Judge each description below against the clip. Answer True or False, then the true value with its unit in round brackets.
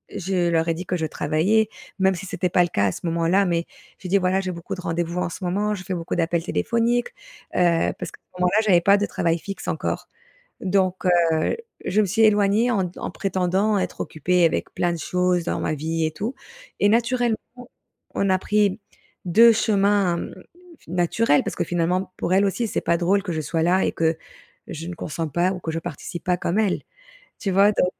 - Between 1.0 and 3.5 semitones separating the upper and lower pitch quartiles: True (2.9 semitones)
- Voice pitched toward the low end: False (180 Hz)